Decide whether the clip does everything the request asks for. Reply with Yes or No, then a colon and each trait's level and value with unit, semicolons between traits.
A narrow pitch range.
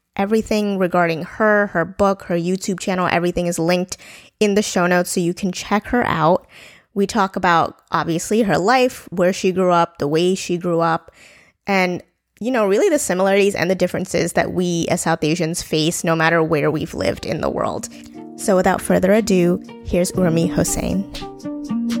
No: average, 3.0 semitones